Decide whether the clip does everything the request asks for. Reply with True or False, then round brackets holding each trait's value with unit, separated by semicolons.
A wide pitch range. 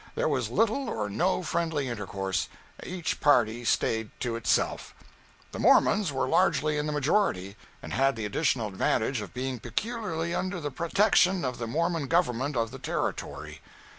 True (6.9 semitones)